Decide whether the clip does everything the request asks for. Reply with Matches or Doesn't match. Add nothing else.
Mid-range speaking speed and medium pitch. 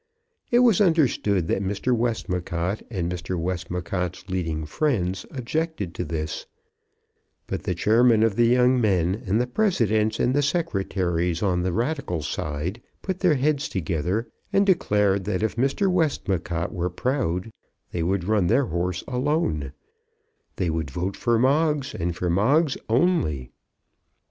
Doesn't match